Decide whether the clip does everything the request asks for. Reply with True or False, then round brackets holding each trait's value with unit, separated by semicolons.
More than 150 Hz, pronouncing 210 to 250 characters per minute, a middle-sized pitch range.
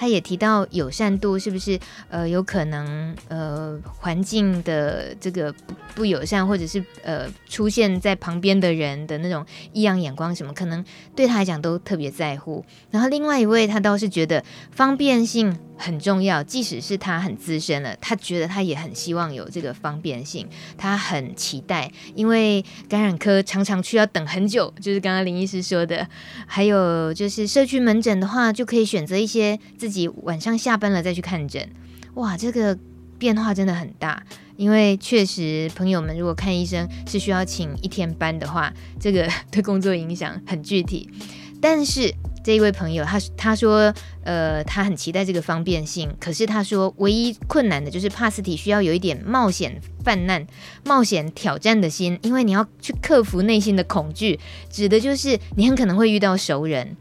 False (190 Hz; 275 characters per minute; 4.3 semitones)